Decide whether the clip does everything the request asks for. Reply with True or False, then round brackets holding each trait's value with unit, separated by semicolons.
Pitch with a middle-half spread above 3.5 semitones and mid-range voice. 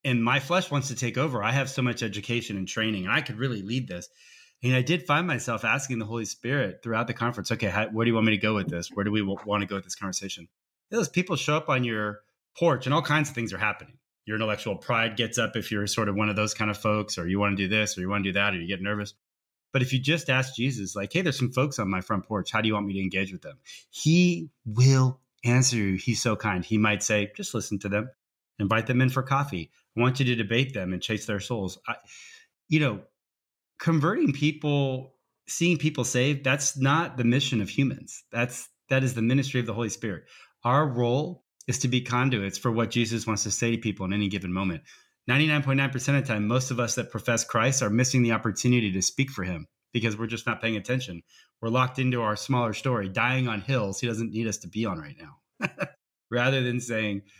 False (3.9 semitones; 120 Hz)